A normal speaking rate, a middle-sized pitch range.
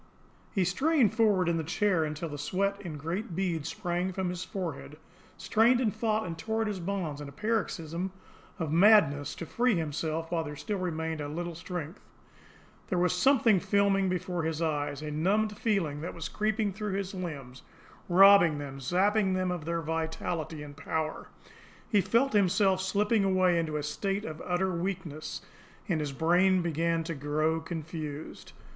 Yes: average, 170 wpm; average, 3.9 semitones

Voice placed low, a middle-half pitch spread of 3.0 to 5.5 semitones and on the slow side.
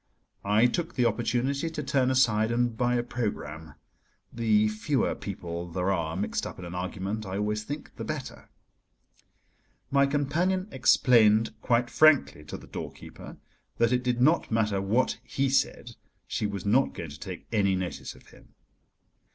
No: low, 115 Hz; average, 4.6 semitones; average, 160 wpm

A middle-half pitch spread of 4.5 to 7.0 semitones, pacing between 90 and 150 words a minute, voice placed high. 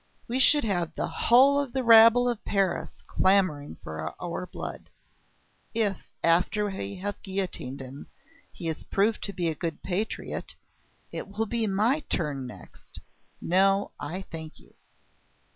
Yes: average, 5.2 semitones; average, 145 wpm; high, 195 Hz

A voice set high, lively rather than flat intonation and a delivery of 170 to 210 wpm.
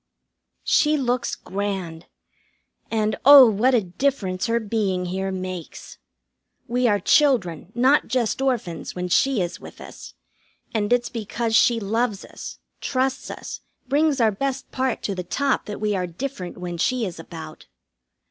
No: high, 220 Hz; wide, 5.7 semitones; average, 150 wpm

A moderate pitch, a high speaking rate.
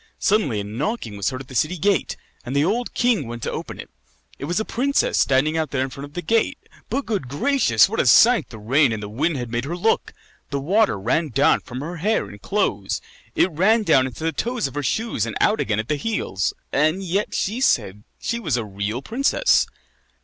Yes: medium, 145 Hz; fast, 230 wpm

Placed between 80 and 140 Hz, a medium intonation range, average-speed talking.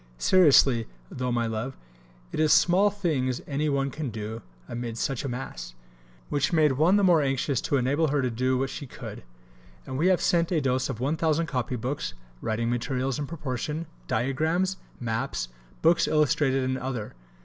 Yes: low, 135 Hz; average, 4.0 semitones; average, 170 wpm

